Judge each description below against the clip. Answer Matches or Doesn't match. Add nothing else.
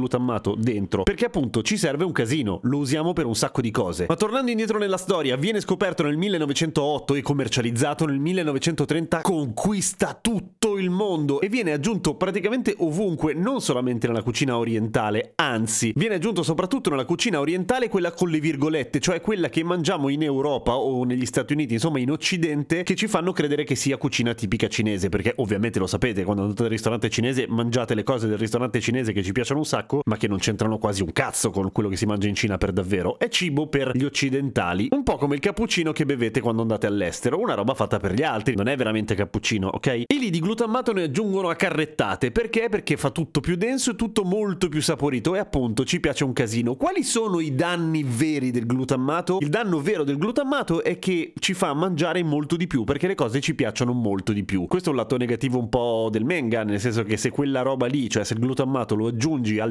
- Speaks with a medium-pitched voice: Matches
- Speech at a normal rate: Doesn't match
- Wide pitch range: Matches